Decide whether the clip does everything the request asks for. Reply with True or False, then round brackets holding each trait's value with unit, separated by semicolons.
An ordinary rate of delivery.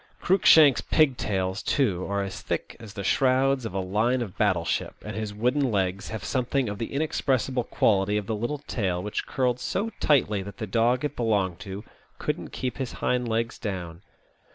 True (185 wpm)